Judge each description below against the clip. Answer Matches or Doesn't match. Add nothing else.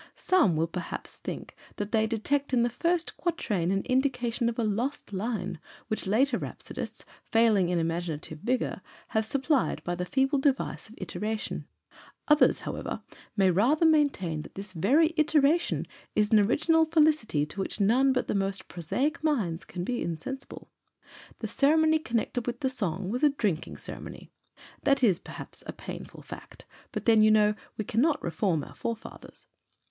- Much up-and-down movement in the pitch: Matches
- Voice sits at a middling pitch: Doesn't match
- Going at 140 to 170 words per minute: Matches